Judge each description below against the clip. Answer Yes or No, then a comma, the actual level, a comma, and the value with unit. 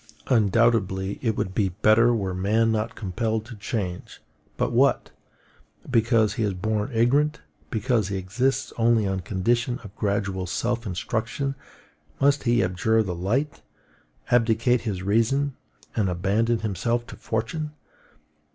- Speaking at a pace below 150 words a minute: Yes, slow, 135 wpm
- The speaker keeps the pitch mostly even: No, average, 3.3 semitones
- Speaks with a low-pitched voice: Yes, low, 110 Hz